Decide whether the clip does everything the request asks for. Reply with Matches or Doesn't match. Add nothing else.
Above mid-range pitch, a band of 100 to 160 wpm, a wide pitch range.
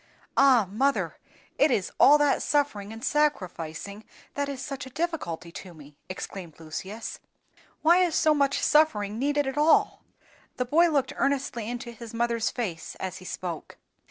Matches